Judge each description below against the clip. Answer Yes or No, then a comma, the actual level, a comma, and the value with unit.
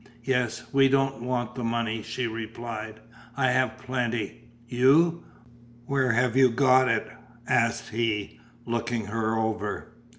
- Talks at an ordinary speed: No, slow, 130 wpm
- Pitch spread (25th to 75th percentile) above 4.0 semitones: No, narrow, 2.4 semitones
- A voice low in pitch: Yes, low, 120 Hz